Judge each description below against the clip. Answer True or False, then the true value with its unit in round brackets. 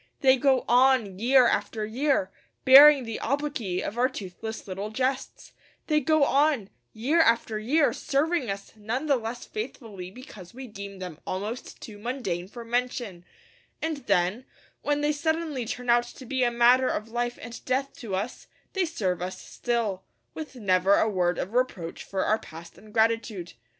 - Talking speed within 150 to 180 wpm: True (165 wpm)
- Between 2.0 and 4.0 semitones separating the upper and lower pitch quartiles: False (4.8 semitones)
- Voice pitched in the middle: False (235 Hz)